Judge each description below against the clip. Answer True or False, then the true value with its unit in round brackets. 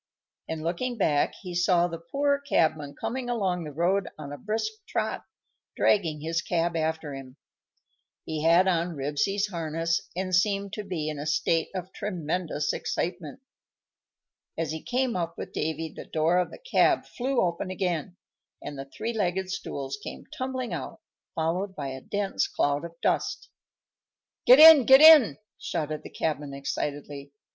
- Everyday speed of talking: True (160 wpm)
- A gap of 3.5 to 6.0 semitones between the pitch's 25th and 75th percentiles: True (4.4 semitones)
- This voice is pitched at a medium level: True (170 Hz)